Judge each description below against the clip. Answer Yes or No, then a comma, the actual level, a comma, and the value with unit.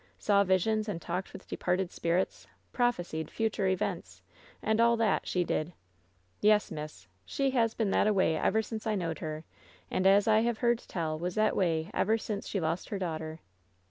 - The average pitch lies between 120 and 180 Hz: No, high, 190 Hz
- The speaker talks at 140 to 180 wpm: No, average, 190 wpm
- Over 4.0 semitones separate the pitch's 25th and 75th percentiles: Yes, average, 4.6 semitones